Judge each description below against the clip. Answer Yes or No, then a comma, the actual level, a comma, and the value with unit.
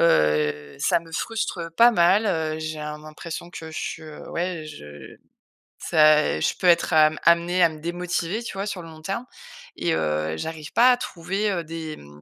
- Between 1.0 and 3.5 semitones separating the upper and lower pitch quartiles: Yes, average, 2.7 semitones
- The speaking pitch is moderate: Yes, medium, 165 Hz